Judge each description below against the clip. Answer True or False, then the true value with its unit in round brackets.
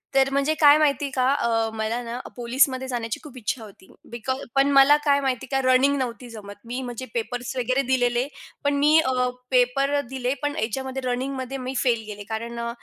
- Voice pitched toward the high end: True (255 Hz)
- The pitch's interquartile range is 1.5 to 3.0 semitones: True (2.4 semitones)